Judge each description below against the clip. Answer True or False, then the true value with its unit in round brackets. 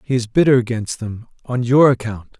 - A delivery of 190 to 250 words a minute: True (200 wpm)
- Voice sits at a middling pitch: False (120 Hz)